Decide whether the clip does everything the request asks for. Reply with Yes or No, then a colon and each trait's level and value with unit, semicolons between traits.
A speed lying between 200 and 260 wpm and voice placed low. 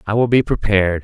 Yes: fast, 230 wpm; low, 105 Hz